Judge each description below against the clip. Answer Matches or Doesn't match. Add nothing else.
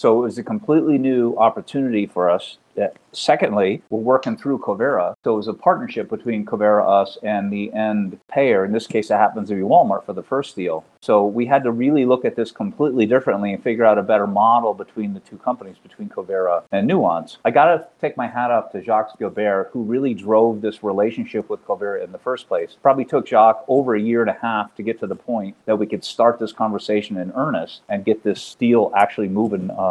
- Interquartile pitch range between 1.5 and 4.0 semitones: Matches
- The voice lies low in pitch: Matches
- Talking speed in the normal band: Doesn't match